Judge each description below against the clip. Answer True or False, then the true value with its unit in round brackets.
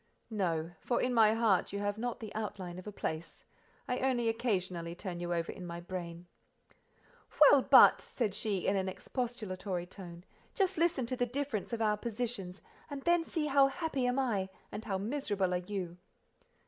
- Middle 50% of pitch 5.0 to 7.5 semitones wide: True (5.3 semitones)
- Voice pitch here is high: True (210 Hz)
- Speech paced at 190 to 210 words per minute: False (180 wpm)